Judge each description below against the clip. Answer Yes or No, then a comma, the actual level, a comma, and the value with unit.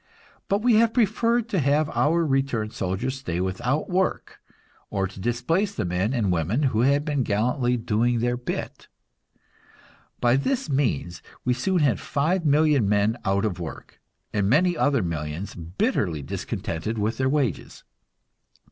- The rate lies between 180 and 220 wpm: No, average, 150 wpm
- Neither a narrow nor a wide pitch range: No, wide, 7.0 semitones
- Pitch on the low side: Yes, low, 125 Hz